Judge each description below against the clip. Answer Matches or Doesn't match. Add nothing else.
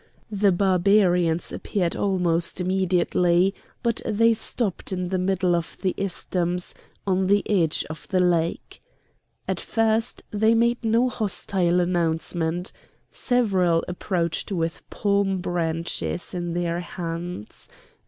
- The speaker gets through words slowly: Matches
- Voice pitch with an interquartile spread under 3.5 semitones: Matches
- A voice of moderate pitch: Matches